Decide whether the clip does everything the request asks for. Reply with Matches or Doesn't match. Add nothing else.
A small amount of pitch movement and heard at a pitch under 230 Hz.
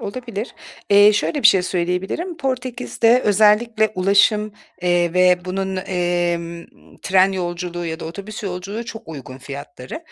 Doesn't match